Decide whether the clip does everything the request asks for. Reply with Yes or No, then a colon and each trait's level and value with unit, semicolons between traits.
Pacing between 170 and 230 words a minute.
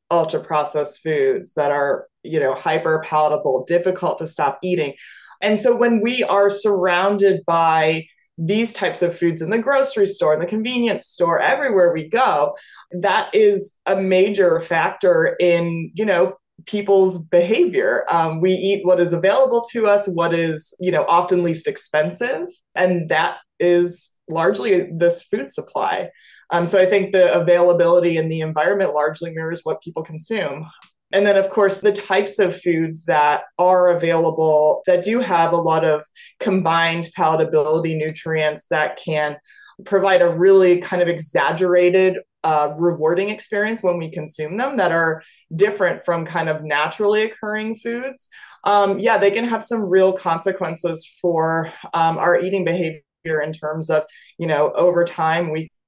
No: average, 155 wpm